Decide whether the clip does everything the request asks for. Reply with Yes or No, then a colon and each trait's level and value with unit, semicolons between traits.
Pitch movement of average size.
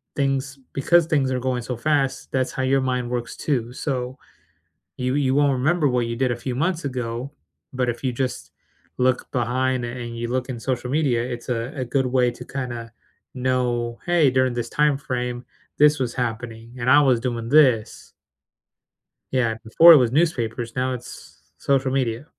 No: narrow, 2.1 semitones